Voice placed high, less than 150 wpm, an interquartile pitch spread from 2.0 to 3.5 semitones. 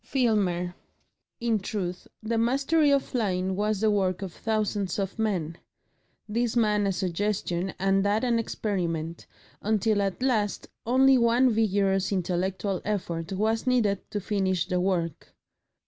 Yes: high, 205 Hz; slow, 135 wpm; average, 3.2 semitones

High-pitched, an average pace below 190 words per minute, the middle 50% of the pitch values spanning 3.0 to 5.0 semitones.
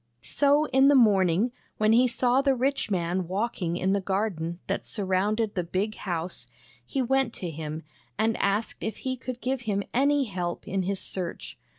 No: high, 210 Hz; average, 180 wpm; wide, 5.4 semitones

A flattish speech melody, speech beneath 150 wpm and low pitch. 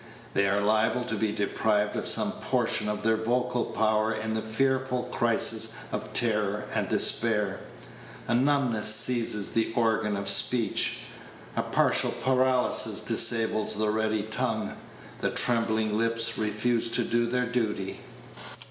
Yes: narrow, 2.0 semitones; average, 140 wpm; low, 110 Hz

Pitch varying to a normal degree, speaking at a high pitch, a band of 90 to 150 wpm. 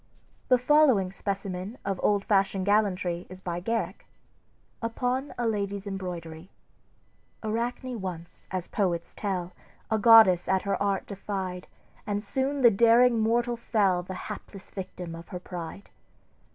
Yes: average, 3.8 semitones; high, 200 Hz; slow, 135 wpm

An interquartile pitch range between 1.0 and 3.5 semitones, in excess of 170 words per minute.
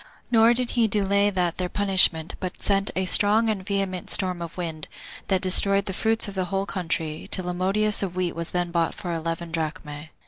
Yes: average, 2.8 semitones; fast, 205 wpm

